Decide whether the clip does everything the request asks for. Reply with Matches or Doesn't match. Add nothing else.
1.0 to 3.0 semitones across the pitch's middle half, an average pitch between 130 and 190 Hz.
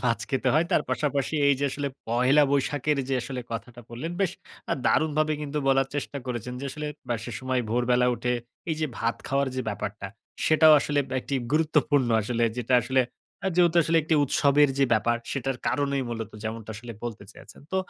Doesn't match